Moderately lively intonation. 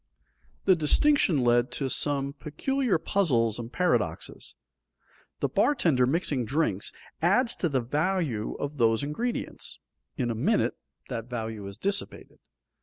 No: wide, 7.2 semitones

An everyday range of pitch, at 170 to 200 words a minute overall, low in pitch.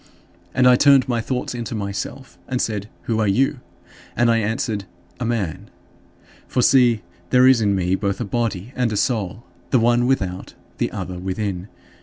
Yes: average, 3.9 semitones; average, 175 wpm; low, 115 Hz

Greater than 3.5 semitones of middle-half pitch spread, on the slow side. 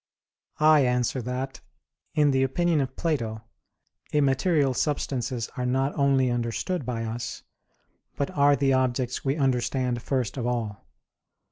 No: narrow, 2.5 semitones; slow, 130 wpm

